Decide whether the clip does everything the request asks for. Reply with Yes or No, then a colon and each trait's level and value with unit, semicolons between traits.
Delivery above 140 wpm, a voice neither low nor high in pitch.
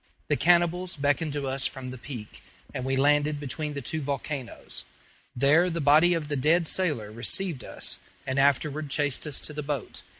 Yes: average, 180 wpm; medium, 145 Hz